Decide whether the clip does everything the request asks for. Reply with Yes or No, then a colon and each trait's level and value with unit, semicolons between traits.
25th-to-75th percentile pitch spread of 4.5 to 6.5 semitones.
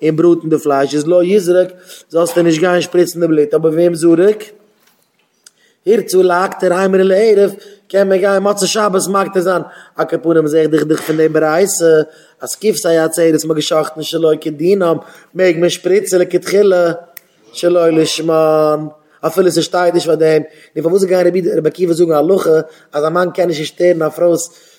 No: average, 2.8 semitones